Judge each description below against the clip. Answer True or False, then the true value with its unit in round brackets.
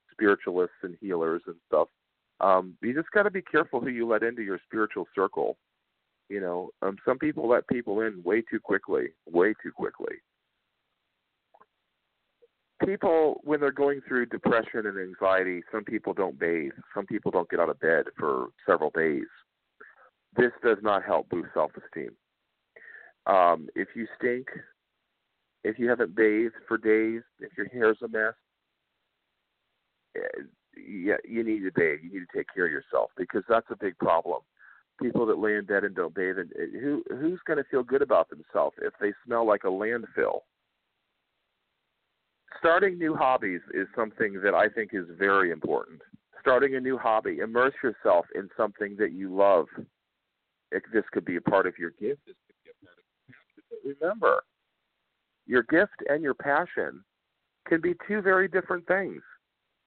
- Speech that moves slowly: False (160 wpm)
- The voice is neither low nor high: False (125 Hz)